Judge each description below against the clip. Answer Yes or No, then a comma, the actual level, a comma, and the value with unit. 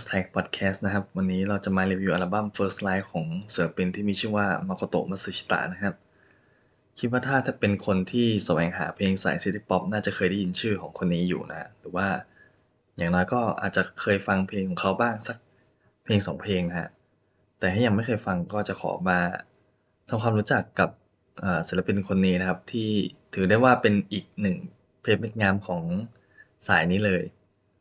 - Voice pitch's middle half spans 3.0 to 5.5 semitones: No, narrow, 2.5 semitones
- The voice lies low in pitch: Yes, low, 100 Hz